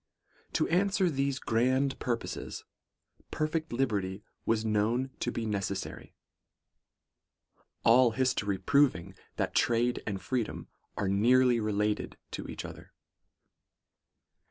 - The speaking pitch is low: Yes, low, 120 Hz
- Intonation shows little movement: No, average, 4.0 semitones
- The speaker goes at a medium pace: No, slow, 110 wpm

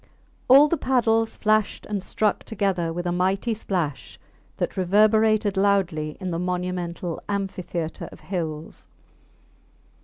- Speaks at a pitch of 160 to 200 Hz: Yes, high, 190 Hz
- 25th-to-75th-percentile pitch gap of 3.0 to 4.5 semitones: Yes, average, 3.6 semitones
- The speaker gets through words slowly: Yes, slow, 120 wpm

